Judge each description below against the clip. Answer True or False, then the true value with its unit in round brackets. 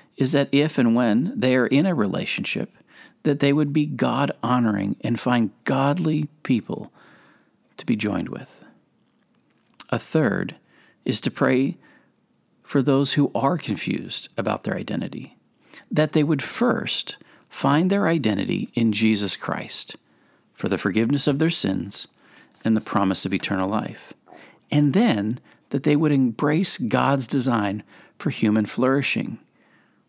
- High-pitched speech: False (135 Hz)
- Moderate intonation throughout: True (4.7 semitones)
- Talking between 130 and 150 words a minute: True (140 wpm)